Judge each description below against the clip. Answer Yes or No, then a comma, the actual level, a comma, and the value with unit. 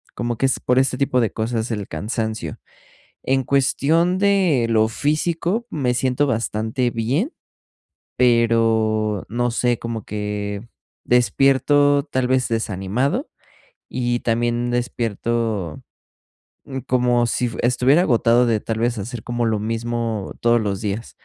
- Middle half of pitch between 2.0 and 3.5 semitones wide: Yes, average, 2.8 semitones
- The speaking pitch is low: Yes, low, 120 Hz